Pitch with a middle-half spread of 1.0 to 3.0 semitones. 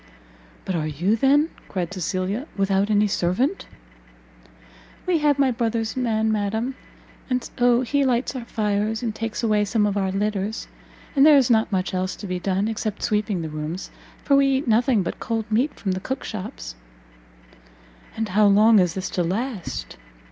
No: average, 4.1 semitones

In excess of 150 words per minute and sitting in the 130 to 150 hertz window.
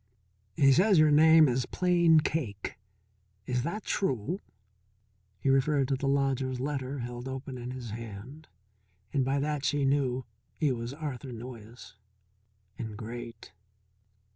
No: slow, 135 wpm; low, 135 Hz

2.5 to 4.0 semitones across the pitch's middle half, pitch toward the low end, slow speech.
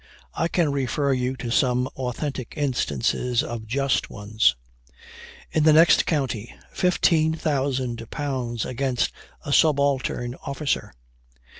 Yes: average, 3.2 semitones; low, 130 Hz; slow, 105 wpm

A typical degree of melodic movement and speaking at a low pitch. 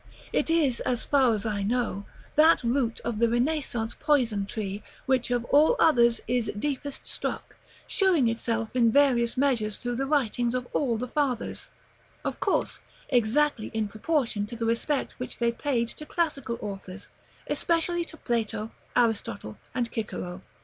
No: average, 4.1 semitones; high, 240 Hz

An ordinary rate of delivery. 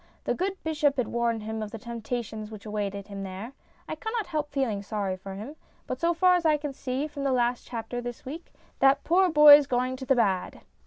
No: fast, 220 wpm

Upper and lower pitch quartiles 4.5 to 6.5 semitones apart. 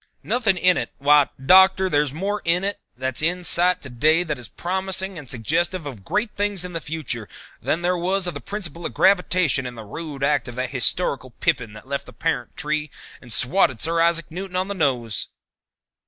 Yes: average, 5.3 semitones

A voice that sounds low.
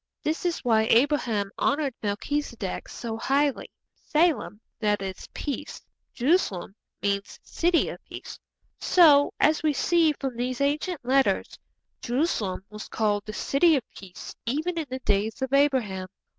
No: very high, 260 Hz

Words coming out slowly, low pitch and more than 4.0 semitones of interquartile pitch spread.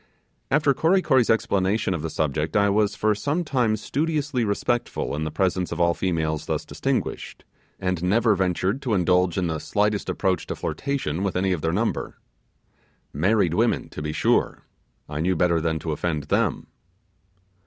No: average, 170 wpm; very low, 95 Hz; average, 5.3 semitones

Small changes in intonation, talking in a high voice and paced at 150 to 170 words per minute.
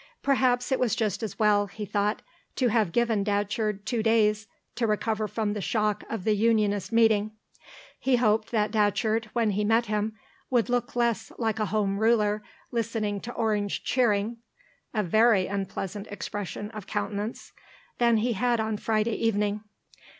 Yes: narrow, 1.8 semitones; high, 215 Hz; average, 160 wpm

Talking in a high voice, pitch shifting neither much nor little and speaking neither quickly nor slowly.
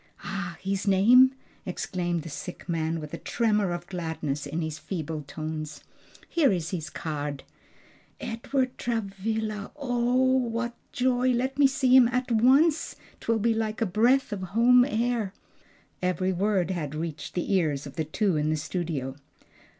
No: high, 195 Hz; wide, 6.8 semitones; average, 155 wpm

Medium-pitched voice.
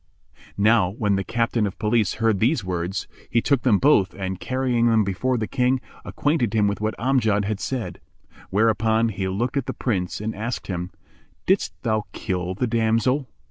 No: low, 110 Hz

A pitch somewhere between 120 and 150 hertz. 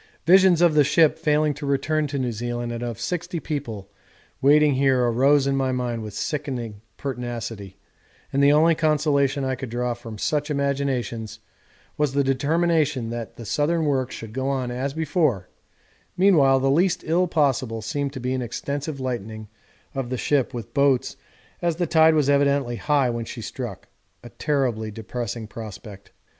Yes: low, 135 Hz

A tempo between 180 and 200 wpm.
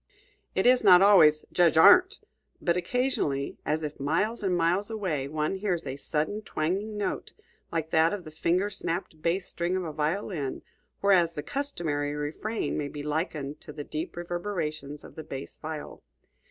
No: average, 165 wpm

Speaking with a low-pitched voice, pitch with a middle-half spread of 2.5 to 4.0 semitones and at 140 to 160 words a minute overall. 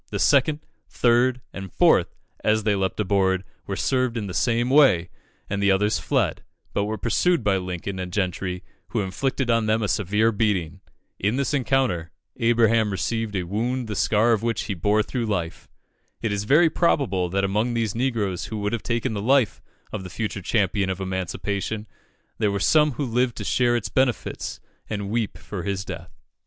No: low, 105 Hz; average, 3.6 semitones; average, 185 wpm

